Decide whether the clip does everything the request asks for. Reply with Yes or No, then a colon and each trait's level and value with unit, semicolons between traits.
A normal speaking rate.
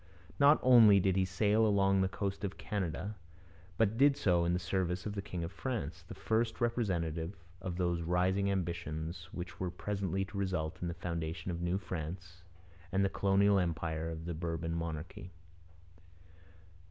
Yes: average, 165 wpm